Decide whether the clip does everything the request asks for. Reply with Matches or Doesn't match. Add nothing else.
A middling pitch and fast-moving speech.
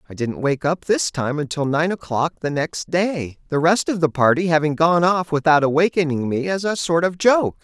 Matches